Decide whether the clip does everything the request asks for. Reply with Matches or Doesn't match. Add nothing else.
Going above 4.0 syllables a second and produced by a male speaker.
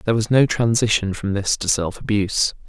Matches